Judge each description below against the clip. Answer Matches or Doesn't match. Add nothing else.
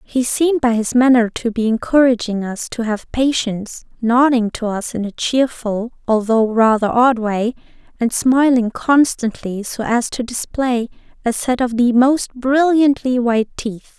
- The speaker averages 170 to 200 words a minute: Doesn't match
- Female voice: Matches